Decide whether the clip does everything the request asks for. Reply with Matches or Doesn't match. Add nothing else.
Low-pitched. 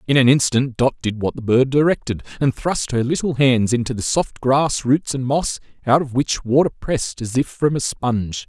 Matches